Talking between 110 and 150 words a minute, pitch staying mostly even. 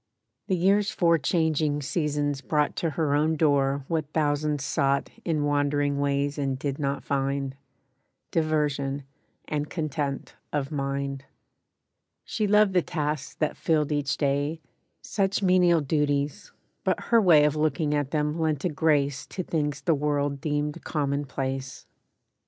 Yes: average, 140 wpm; narrow, 2.0 semitones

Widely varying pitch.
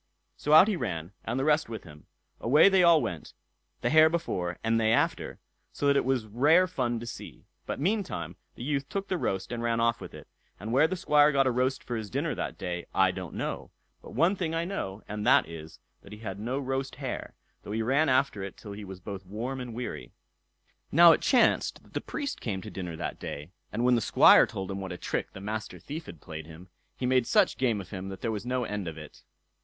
Yes: wide, 6.7 semitones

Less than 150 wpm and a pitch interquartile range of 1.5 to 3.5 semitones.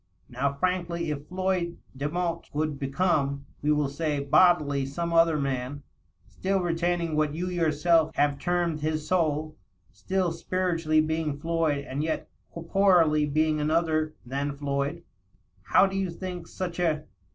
Yes: average, 140 wpm; average, 3.1 semitones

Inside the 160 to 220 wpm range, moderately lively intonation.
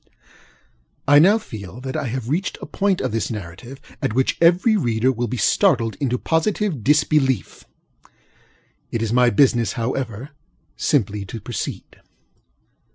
No: average, 140 wpm; average, 4.9 semitones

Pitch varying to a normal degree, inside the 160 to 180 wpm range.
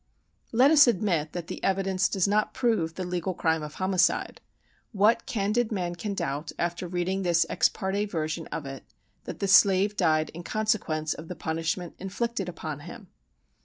Yes: average, 3.8 semitones; average, 170 wpm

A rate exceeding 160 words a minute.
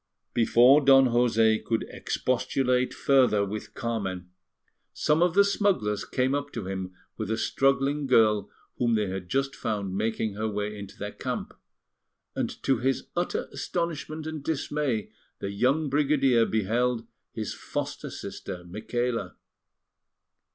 No: slow, 135 wpm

